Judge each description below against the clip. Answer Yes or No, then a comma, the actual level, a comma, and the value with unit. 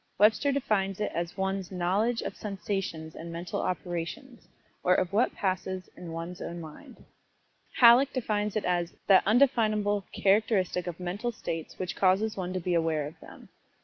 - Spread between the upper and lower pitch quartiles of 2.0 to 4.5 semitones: Yes, average, 3.5 semitones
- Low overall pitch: No, high, 190 Hz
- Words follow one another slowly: No, average, 160 wpm